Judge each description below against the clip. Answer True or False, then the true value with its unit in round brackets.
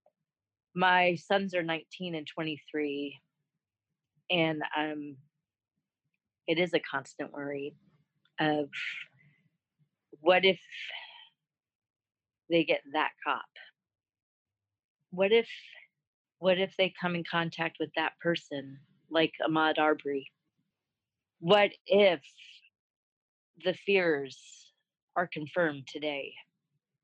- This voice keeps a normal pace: False (90 wpm)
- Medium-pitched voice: True (160 Hz)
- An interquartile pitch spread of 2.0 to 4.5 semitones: True (3.2 semitones)